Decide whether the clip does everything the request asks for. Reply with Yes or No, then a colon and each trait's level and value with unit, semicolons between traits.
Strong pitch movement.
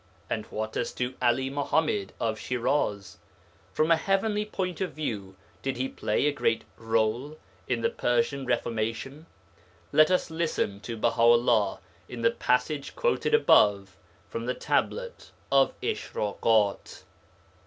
Yes: wide, 5.8 semitones